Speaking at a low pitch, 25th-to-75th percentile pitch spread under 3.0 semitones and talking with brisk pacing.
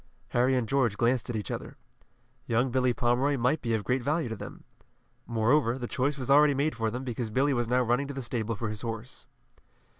Yes: low, 125 Hz; narrow, 2.6 semitones; fast, 215 wpm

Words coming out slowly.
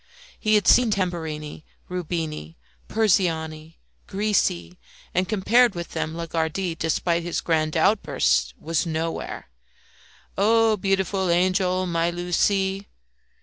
Yes: slow, 105 wpm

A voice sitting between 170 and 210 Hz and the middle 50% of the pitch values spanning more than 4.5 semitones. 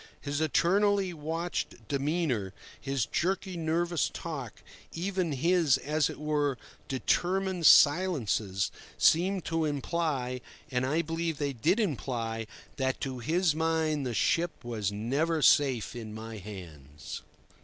No: medium, 150 Hz; average, 5.3 semitones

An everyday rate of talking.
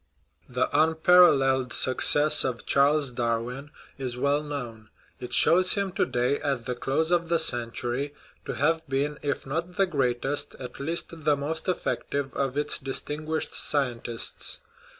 Yes: average, 150 wpm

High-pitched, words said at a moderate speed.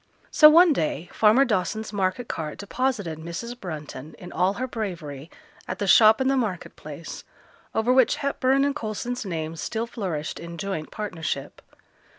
Yes: high, 200 Hz; average, 160 wpm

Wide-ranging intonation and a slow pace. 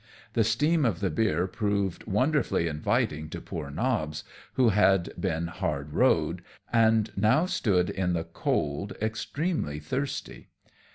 Yes: wide, 5.7 semitones; slow, 130 wpm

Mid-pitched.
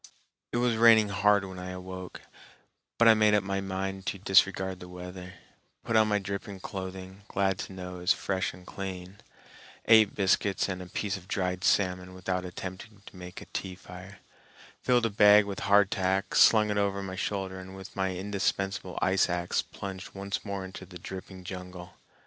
No: very low, 95 Hz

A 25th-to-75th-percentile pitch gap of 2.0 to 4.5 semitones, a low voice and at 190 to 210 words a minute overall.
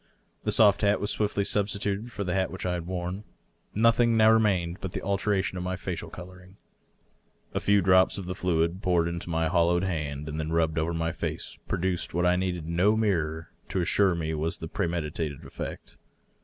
Yes: average, 2.9 semitones; very low, 90 Hz; average, 200 wpm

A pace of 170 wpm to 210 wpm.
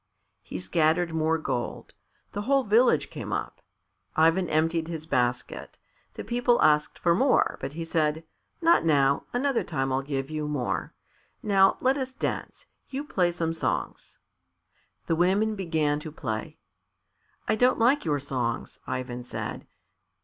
No: average, 145 wpm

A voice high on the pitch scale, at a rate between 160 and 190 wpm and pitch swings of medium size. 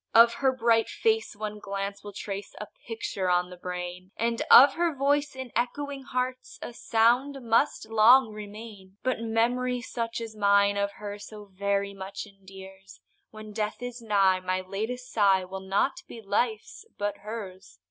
Yes: high, 215 Hz; average, 165 wpm; average, 3.5 semitones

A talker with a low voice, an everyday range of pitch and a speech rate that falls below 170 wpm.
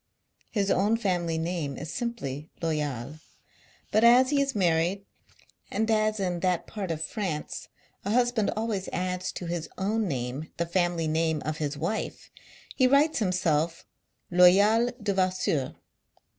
No: medium, 180 Hz; average, 5.0 semitones; average, 140 wpm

